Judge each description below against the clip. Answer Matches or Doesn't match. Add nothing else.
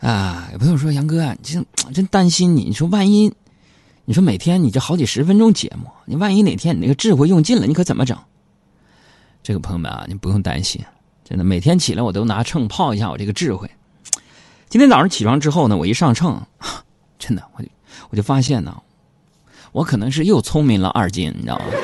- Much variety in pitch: Matches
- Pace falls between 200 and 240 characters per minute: Doesn't match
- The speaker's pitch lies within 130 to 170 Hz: Matches